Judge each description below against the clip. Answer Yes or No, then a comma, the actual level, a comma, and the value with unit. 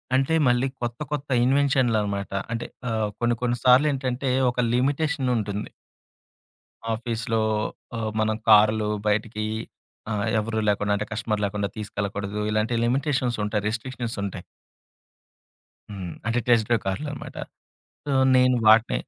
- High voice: No, low, 115 Hz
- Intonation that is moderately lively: Yes, average, 3.2 semitones